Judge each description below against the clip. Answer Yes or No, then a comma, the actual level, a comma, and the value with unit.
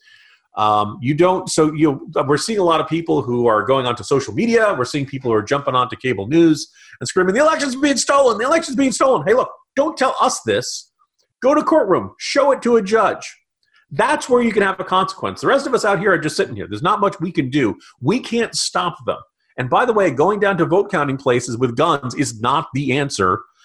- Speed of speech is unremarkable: No, fast, 235 wpm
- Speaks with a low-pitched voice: No, medium, 185 Hz